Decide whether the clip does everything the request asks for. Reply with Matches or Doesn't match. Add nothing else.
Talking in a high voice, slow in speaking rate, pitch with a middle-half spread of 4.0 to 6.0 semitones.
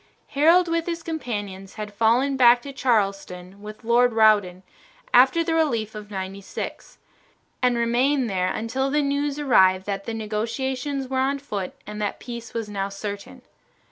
Doesn't match